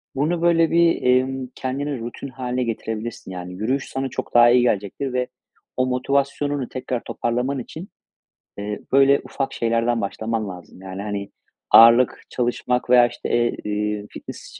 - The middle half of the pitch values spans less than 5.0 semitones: Yes, average, 3.3 semitones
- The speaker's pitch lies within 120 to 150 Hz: Yes, low, 125 Hz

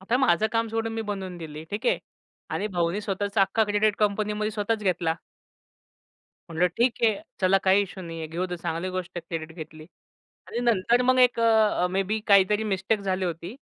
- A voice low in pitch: No, high, 200 Hz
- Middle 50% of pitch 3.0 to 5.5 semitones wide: Yes, average, 3.5 semitones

